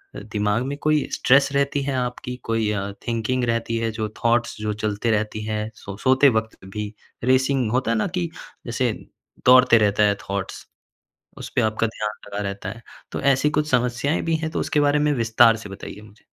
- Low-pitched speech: Yes, low, 115 Hz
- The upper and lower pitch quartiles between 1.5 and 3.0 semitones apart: No, average, 3.6 semitones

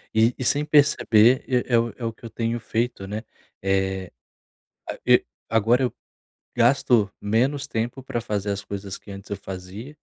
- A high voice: No, low, 115 Hz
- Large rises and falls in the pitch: No, average, 3.4 semitones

